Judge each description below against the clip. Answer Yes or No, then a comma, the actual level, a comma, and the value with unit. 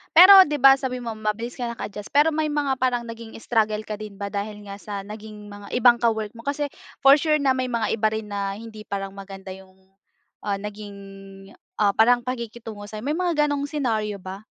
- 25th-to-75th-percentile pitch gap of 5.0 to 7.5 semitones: No, average, 4.0 semitones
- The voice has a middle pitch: No, high, 225 Hz